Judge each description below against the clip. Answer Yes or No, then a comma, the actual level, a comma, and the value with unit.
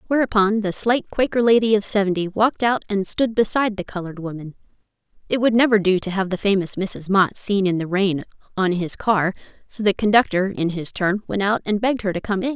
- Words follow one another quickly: Yes, fast, 220 wpm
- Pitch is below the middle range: No, high, 200 Hz